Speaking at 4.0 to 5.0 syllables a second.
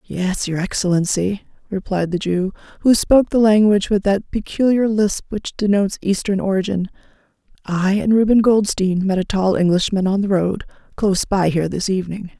No: 5.3 syllables/s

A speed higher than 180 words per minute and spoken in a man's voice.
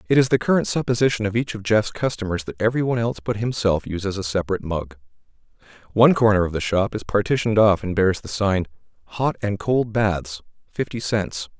Yes: average, 190 wpm; male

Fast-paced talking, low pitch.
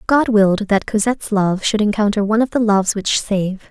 No: fast, 210 wpm; high, 210 Hz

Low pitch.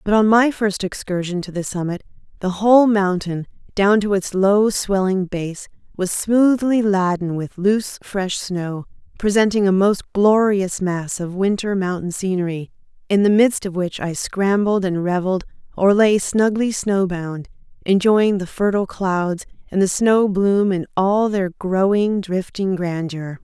No: high, 195 Hz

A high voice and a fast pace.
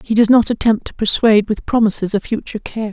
Yes: high, 215 Hz; fast, 225 wpm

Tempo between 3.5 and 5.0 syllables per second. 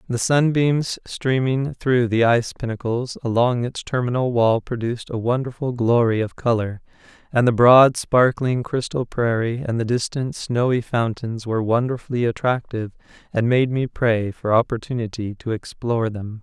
Yes: 4.8 syllables/s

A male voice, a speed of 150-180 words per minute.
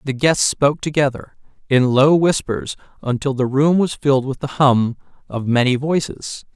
Yes: male; average, 165 wpm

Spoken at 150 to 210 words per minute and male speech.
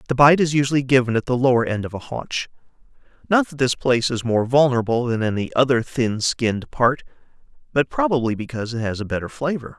Yes: average, 200 wpm; male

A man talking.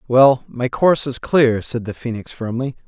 Yes: male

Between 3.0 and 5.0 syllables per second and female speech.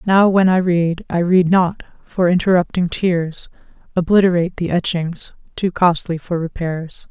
Yes: 4.4 syllables/s; female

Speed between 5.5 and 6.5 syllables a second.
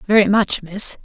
No: 4.4 syllables/s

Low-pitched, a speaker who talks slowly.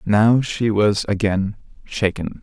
Yes: low, 105 Hz; slow, 125 wpm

